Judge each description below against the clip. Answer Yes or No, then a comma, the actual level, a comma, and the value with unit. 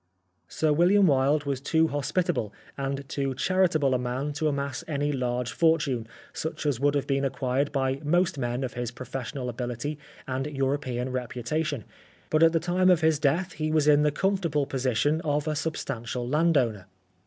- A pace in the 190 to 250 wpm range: No, average, 175 wpm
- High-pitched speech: No, medium, 140 Hz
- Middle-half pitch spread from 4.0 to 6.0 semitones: No, average, 3.4 semitones